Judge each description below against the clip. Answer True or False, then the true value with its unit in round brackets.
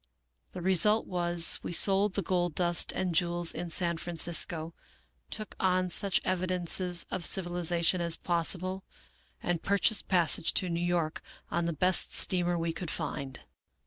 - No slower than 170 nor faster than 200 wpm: False (155 wpm)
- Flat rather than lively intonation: True (1.5 semitones)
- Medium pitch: True (175 Hz)